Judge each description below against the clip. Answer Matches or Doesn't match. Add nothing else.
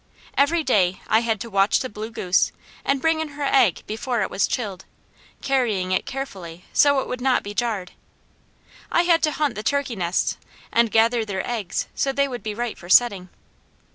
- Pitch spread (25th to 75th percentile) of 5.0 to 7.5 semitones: Matches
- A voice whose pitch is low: Doesn't match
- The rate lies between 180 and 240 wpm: Matches